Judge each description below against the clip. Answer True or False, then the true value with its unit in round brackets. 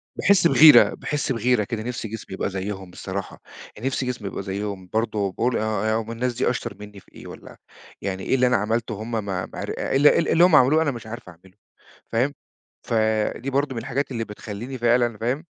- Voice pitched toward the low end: True (115 Hz)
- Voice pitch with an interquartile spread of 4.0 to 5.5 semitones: False (3.5 semitones)